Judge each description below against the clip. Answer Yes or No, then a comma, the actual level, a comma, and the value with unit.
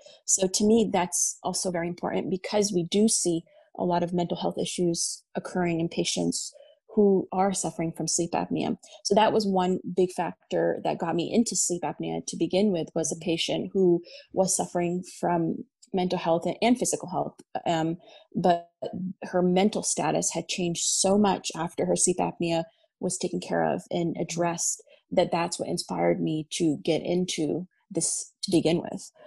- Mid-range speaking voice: Yes, medium, 180 Hz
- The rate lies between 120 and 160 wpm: No, average, 170 wpm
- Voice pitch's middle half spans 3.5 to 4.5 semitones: No, average, 2.7 semitones